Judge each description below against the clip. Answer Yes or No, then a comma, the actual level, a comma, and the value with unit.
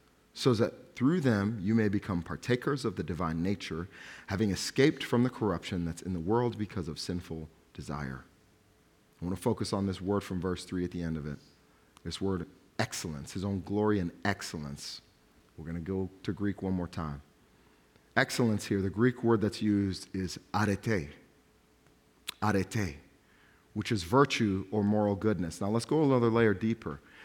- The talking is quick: No, average, 175 wpm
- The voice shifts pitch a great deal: No, average, 4.0 semitones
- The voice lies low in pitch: Yes, low, 100 Hz